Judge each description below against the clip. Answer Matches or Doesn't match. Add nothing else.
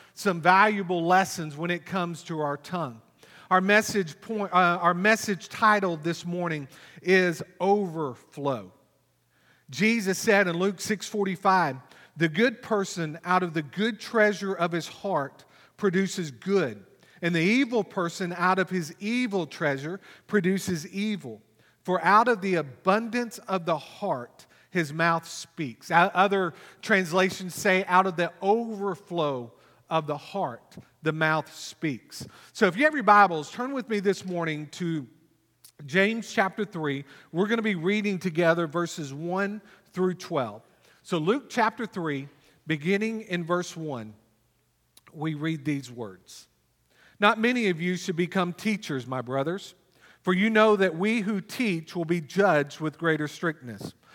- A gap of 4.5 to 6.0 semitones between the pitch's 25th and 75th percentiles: Doesn't match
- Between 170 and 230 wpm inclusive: Doesn't match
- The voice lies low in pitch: Doesn't match